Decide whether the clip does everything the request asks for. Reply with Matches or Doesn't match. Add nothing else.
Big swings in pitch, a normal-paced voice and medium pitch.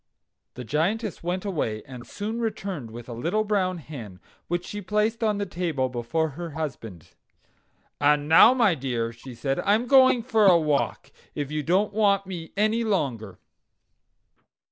Matches